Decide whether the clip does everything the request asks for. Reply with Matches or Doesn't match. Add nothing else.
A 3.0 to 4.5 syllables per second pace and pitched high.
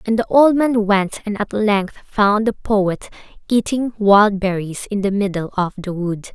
Matches